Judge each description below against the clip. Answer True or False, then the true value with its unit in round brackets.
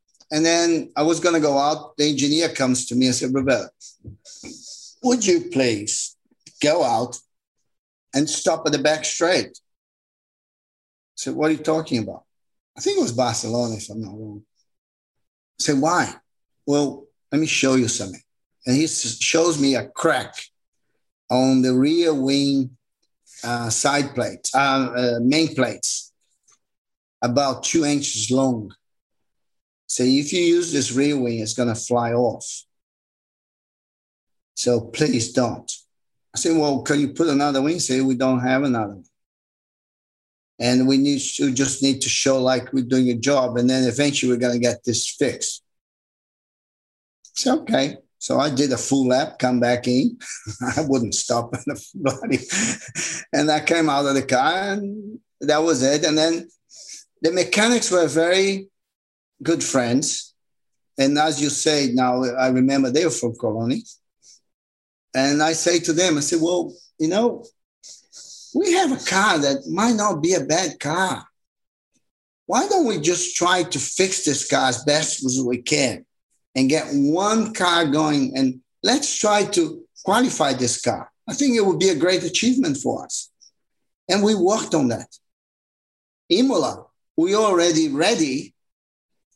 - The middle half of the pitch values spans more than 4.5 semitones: True (5.1 semitones)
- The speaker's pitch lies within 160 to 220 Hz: False (140 Hz)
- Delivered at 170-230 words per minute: False (155 wpm)